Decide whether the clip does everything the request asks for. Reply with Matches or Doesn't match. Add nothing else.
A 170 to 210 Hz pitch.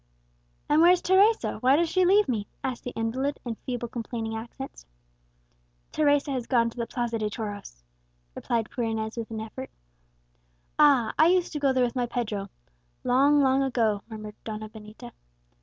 Doesn't match